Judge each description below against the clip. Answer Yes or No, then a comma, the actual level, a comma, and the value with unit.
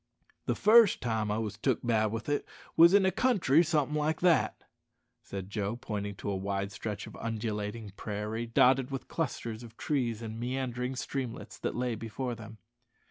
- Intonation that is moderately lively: Yes, average, 4.1 semitones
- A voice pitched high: No, low, 115 Hz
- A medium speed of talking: Yes, average, 175 wpm